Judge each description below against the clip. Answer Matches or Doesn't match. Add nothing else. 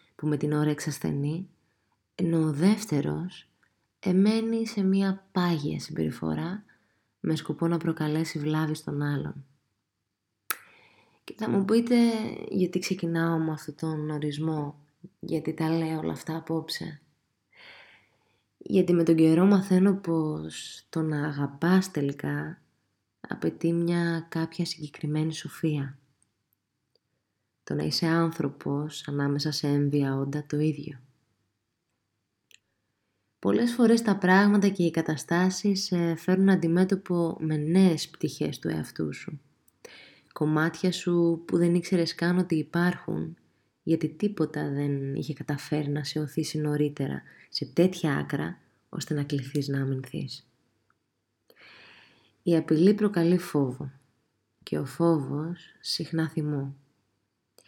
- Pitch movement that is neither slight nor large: Matches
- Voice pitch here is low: Doesn't match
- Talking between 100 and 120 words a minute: Matches